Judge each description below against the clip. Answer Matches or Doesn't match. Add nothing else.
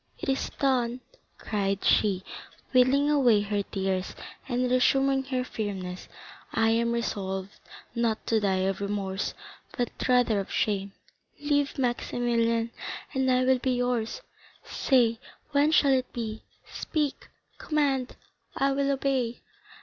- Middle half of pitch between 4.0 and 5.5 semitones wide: Matches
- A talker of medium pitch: Doesn't match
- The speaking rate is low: Matches